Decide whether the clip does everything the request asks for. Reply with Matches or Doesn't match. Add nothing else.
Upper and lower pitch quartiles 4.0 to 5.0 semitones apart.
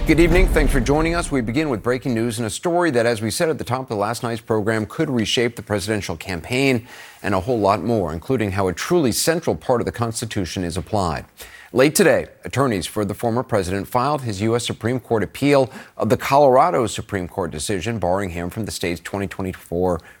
Matches